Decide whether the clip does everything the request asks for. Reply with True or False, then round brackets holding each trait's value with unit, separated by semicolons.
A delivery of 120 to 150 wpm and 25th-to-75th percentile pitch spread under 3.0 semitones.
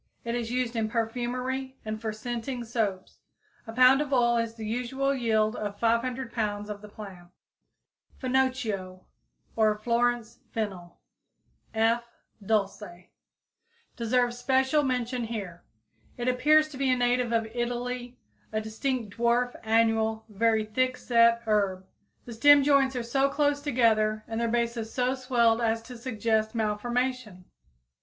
True (145 wpm; 2.5 semitones)